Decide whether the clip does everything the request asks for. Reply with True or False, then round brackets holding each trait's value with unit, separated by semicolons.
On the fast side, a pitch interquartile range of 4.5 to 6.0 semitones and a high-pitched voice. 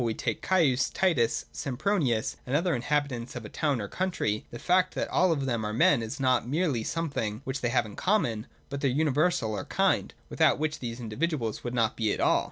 False (215 wpm; 5.2 semitones; 130 Hz)